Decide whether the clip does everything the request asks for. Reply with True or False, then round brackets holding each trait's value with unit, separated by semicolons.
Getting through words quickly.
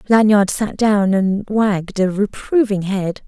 False (145 wpm)